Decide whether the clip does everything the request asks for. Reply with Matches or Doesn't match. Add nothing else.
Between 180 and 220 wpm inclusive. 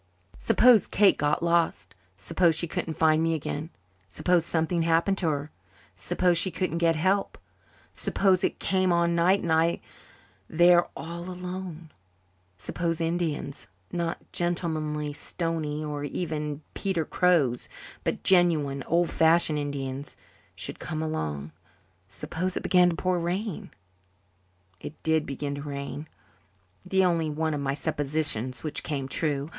Doesn't match